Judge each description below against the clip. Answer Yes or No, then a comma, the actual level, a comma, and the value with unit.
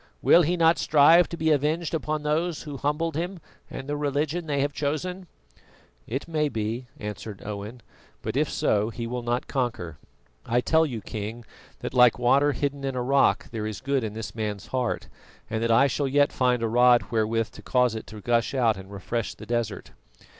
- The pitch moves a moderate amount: Yes, average, 4.7 semitones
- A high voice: No, low, 125 Hz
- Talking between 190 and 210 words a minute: Yes, average, 195 wpm